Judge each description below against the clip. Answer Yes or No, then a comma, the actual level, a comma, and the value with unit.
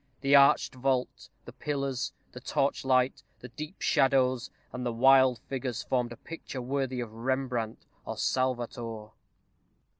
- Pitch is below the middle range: Yes, low, 130 Hz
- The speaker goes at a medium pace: No, slow, 130 wpm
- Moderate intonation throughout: No, narrow, 1.8 semitones